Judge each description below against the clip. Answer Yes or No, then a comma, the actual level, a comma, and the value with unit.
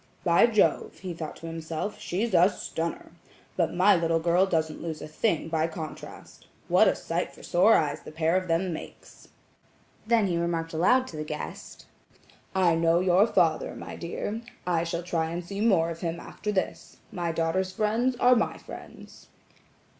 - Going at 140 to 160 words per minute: No, average, 175 wpm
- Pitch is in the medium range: Yes, medium, 170 Hz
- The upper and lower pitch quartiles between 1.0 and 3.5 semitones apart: Yes, average, 2.7 semitones